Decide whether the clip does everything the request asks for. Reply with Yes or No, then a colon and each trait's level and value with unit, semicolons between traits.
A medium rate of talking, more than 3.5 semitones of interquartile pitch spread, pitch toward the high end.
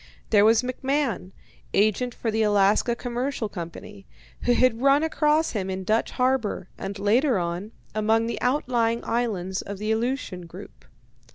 Yes: average, 150 wpm; average, 3.9 semitones; high, 225 Hz